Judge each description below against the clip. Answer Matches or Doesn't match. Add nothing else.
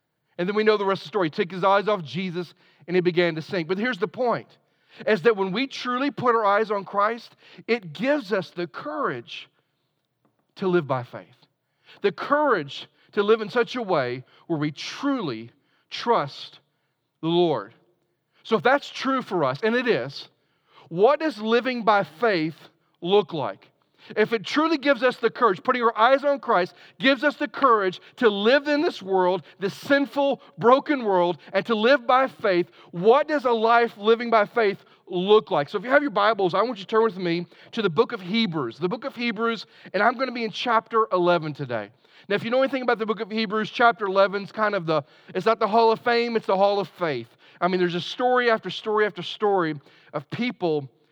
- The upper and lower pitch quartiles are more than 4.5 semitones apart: Matches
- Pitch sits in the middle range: Doesn't match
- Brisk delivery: Matches